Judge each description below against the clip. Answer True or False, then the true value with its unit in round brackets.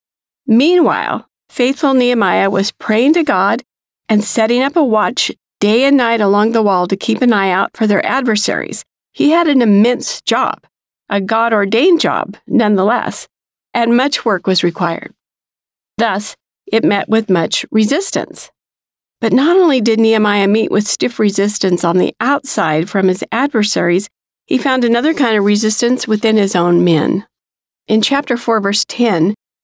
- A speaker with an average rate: True (155 wpm)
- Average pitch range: True (3.8 semitones)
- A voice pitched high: True (225 Hz)